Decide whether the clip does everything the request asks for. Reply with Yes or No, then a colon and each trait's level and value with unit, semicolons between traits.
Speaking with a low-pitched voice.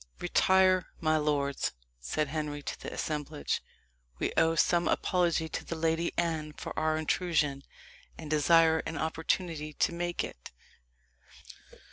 No: medium, 160 Hz